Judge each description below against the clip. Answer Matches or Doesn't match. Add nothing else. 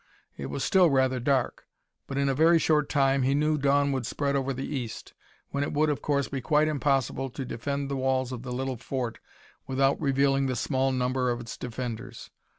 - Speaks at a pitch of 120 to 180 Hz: Matches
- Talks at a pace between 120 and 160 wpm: Doesn't match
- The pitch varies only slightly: Matches